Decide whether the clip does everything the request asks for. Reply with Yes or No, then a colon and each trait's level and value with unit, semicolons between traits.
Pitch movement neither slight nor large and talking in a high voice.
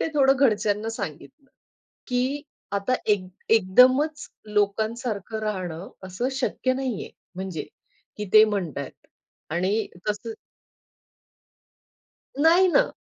Yes: average, 4.7 semitones; high, 215 Hz